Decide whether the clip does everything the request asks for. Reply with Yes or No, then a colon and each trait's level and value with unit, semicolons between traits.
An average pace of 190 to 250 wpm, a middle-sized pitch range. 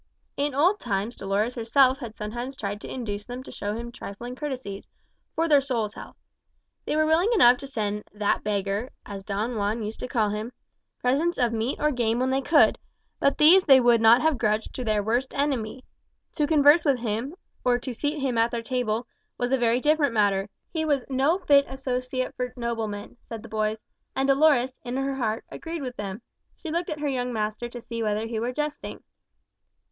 Yes: fast, 205 wpm; average, 4.1 semitones